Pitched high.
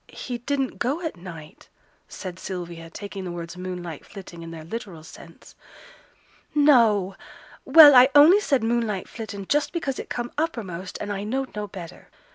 Yes: high, 205 Hz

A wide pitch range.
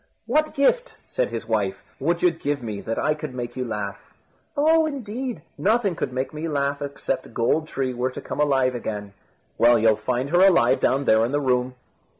Yes: wide, 7.9 semitones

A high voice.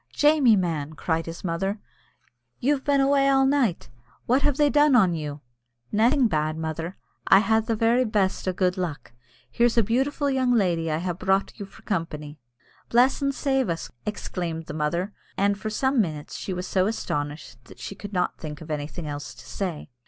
Yes: high, 195 Hz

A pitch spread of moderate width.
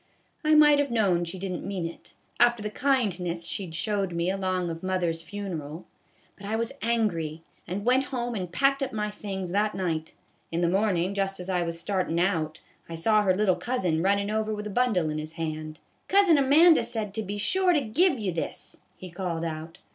Yes: average, 4.7 semitones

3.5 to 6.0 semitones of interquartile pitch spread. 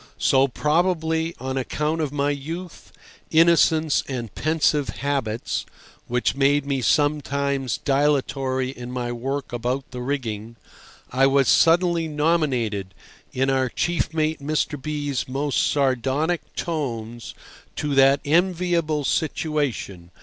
No: average, 3.1 semitones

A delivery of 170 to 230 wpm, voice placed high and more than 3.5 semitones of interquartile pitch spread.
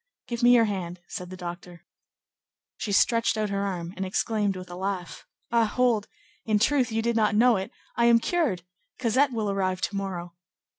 Yes: average, 190 wpm; high, 205 Hz; average, 3.9 semitones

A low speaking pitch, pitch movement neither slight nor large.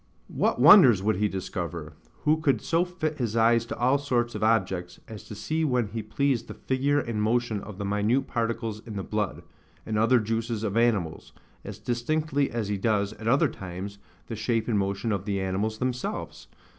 Yes: low, 115 Hz; average, 3.5 semitones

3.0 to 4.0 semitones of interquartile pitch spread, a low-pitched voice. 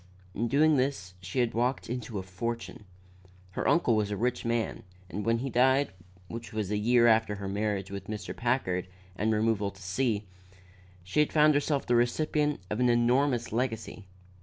Yes: average, 3.4 semitones; low, 115 Hz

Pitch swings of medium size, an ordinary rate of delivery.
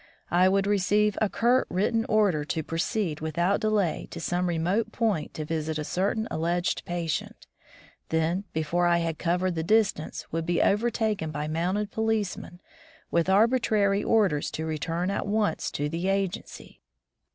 Yes: average, 4.2 semitones; average, 155 wpm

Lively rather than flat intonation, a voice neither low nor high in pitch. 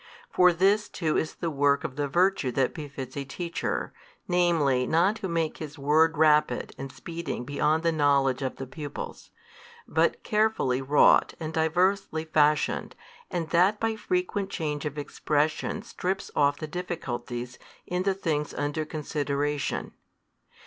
No: average, 3.7 semitones; medium, 155 Hz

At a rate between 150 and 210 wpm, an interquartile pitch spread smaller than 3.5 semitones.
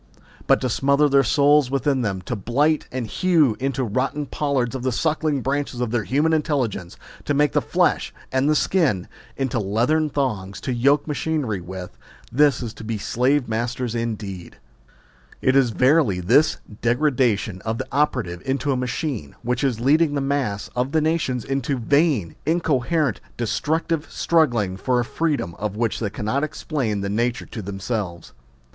No: average, 160 wpm; average, 4.6 semitones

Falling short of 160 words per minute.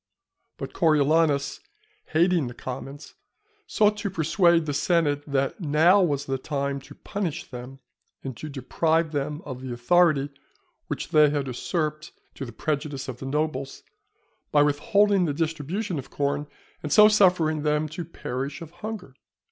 Yes: average, 150 wpm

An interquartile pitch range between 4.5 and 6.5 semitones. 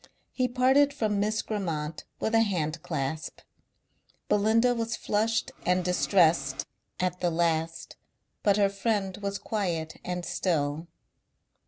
Yes: average, 5.0 semitones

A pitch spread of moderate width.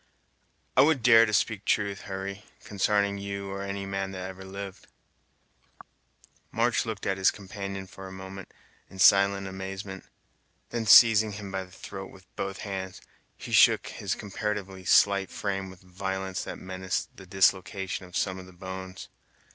No: narrow, 1.0 semitones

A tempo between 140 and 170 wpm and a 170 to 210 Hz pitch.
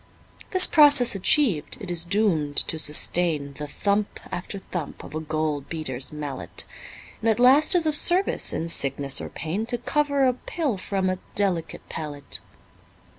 Yes: average, 160 wpm; medium, 185 Hz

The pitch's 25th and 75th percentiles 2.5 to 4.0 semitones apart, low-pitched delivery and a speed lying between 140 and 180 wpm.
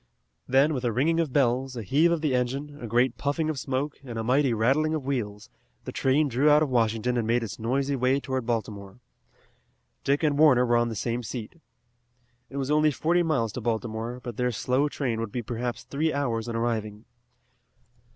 No: average, 3.6 semitones; low, 125 Hz; average, 200 wpm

